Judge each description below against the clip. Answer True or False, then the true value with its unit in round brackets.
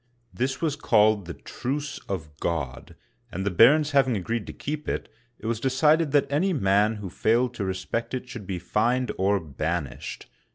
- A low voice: True (115 Hz)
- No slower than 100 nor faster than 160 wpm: False (190 wpm)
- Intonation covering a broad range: True (6.1 semitones)